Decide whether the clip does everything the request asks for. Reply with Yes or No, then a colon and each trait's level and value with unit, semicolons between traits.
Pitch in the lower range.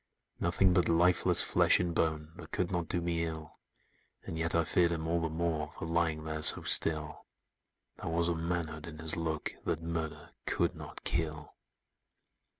Yes: very low, 80 Hz